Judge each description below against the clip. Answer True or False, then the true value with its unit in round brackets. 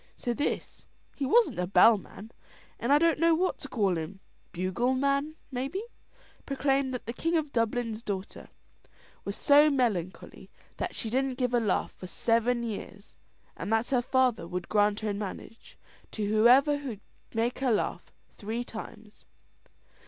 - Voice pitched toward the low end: False (235 Hz)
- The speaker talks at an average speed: True (155 wpm)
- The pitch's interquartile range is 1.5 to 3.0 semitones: False (4.6 semitones)